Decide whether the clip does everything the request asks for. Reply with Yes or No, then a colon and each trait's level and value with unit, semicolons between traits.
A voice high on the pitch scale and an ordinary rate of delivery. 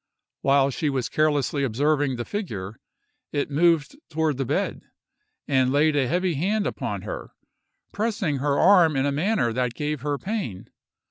No: medium, 145 Hz; average, 155 wpm